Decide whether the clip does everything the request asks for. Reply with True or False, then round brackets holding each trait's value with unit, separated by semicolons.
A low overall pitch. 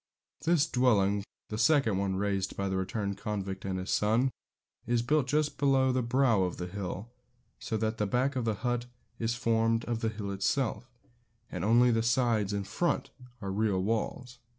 True (115 Hz)